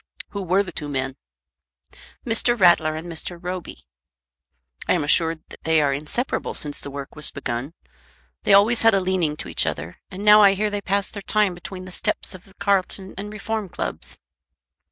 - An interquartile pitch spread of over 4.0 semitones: Yes, average, 4.4 semitones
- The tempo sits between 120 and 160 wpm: No, average, 190 wpm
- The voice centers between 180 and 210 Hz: Yes, medium, 185 Hz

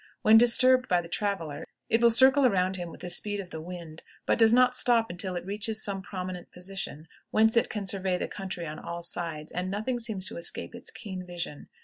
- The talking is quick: Yes, fast, 220 wpm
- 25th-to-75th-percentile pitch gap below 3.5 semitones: No, average, 4.1 semitones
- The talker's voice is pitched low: No, high, 190 Hz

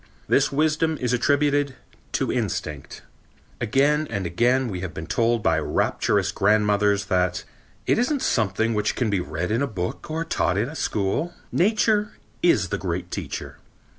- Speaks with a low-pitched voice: Yes, low, 110 Hz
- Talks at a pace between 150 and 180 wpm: Yes, average, 160 wpm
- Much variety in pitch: Yes, wide, 7.6 semitones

